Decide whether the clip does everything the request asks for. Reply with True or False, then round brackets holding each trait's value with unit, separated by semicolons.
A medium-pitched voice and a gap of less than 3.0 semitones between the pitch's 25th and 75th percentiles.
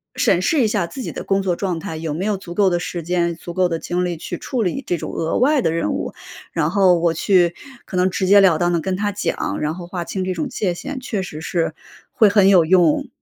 True (180 Hz; 2.6 semitones)